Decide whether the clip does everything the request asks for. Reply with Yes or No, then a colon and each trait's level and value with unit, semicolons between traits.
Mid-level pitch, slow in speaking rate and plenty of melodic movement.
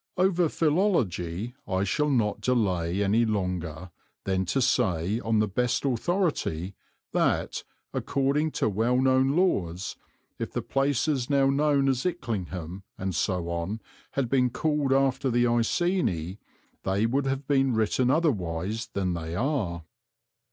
No: low, 120 Hz; slow, 130 wpm; wide, 6.6 semitones